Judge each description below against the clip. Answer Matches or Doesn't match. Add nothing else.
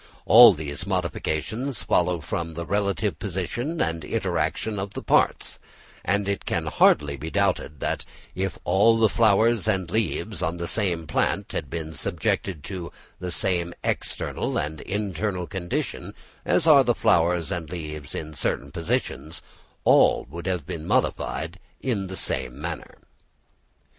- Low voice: Matches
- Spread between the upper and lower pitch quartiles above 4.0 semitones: Doesn't match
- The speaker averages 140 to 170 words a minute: Matches